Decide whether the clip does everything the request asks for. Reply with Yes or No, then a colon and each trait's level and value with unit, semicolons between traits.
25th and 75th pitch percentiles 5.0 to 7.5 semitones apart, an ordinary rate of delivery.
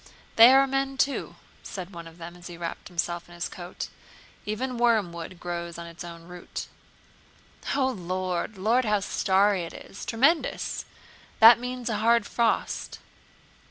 Yes: wide, 5.4 semitones; average, 160 wpm